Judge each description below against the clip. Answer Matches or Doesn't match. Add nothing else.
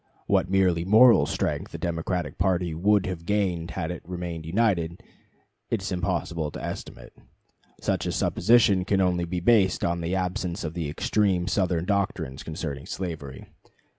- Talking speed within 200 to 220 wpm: Doesn't match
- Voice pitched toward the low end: Matches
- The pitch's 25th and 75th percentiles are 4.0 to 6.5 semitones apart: Doesn't match